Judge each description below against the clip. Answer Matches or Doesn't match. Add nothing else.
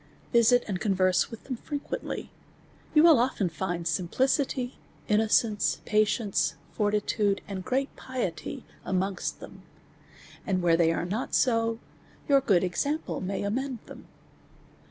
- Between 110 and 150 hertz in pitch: Doesn't match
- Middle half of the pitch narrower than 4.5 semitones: Doesn't match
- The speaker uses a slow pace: Matches